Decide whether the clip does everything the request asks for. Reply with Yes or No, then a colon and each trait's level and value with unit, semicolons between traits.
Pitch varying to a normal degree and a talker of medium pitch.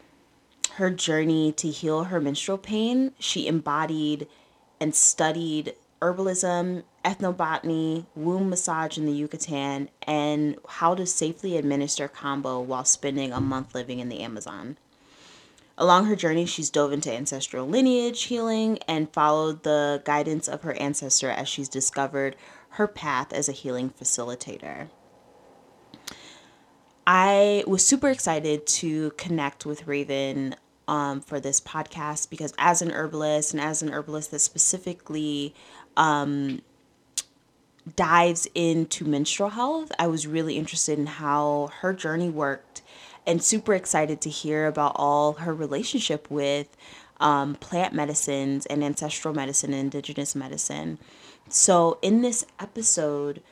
Yes: average, 3.1 semitones; medium, 155 Hz